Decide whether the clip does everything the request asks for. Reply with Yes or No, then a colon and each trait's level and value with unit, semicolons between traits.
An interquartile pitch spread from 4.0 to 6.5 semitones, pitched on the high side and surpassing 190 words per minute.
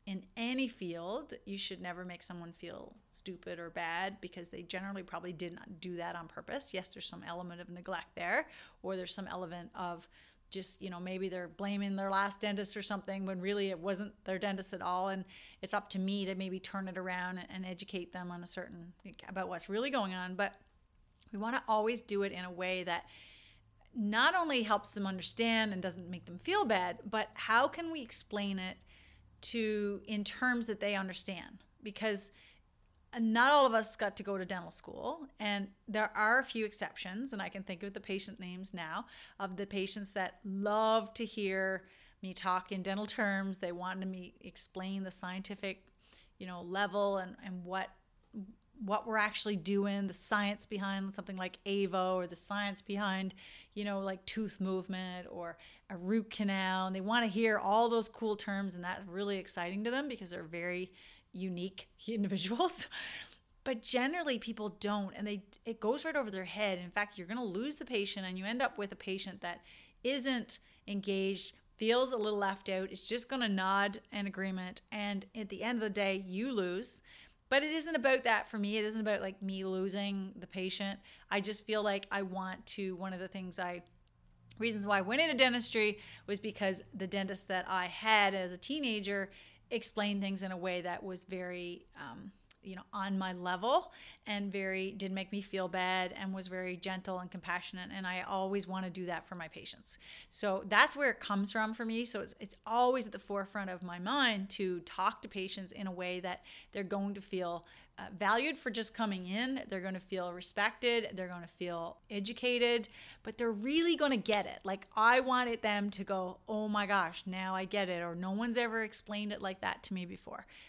No: narrow, 2.5 semitones; high, 195 Hz; average, 200 wpm